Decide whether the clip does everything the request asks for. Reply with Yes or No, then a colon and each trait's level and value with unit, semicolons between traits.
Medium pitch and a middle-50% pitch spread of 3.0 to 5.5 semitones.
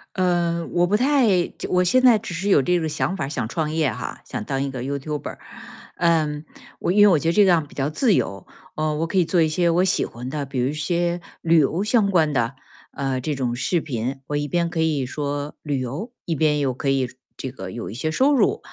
Yes: medium, 155 Hz; average, 4.4 semitones